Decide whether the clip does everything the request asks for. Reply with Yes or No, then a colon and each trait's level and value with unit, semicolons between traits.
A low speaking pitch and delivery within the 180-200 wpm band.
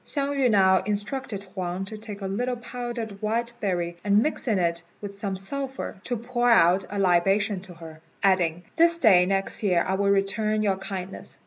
No: high, 200 Hz; average, 185 wpm